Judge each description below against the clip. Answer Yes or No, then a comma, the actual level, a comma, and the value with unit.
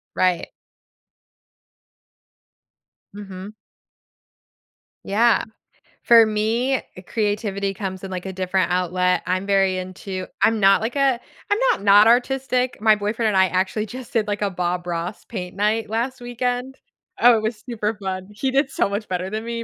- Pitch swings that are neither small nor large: Yes, average, 3.6 semitones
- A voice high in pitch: Yes, high, 210 Hz